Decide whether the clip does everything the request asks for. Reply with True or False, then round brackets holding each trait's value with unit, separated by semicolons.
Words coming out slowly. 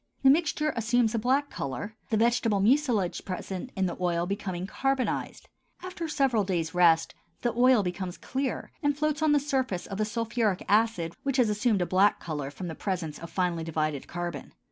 False (185 wpm)